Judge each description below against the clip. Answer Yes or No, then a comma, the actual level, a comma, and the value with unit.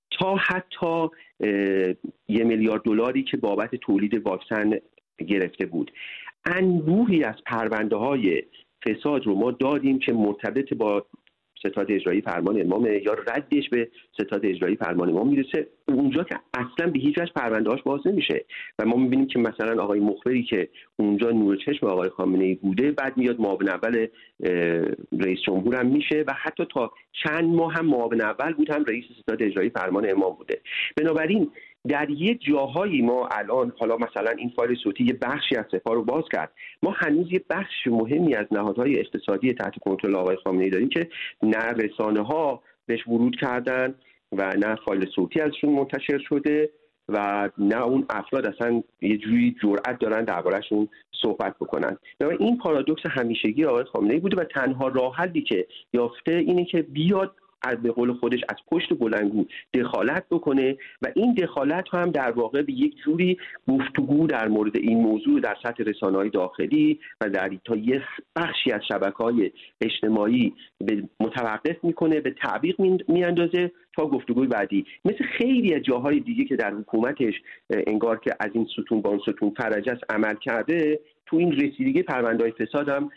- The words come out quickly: Yes, fast, 160 wpm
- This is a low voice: Yes, low, 125 Hz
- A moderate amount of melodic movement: No, wide, 7.0 semitones